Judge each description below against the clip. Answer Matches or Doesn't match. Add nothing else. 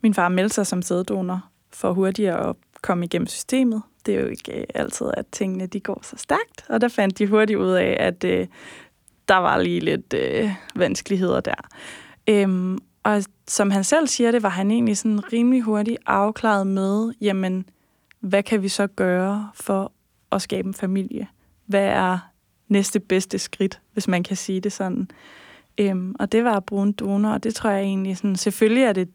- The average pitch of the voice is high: Matches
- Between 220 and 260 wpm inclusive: Doesn't match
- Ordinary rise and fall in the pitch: Doesn't match